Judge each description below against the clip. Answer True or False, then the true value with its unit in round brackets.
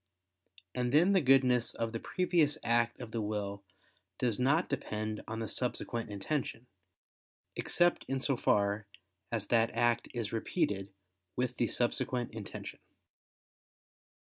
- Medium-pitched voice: False (120 Hz)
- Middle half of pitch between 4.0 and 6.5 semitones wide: False (3.3 semitones)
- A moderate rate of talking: False (130 wpm)